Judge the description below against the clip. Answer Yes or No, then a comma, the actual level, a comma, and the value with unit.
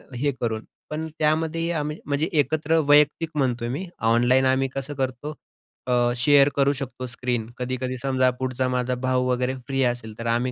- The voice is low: Yes, low, 130 Hz